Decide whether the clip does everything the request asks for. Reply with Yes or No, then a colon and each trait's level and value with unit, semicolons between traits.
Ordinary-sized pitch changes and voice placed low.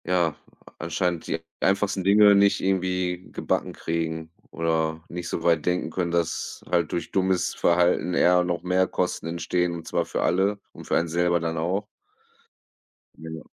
No: narrow, 1.8 semitones; very low, 90 Hz